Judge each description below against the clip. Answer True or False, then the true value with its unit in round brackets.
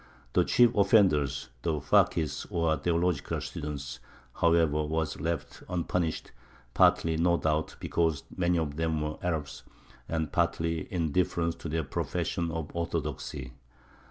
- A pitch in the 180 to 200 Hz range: False (80 Hz)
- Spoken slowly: True (130 wpm)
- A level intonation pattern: True (2.0 semitones)